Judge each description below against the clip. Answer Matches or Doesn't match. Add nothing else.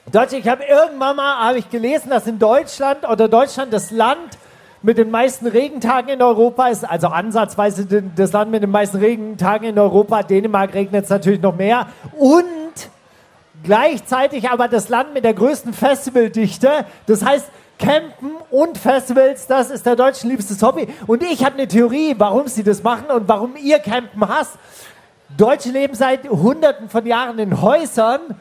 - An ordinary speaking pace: Matches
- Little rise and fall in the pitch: Doesn't match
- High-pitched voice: Matches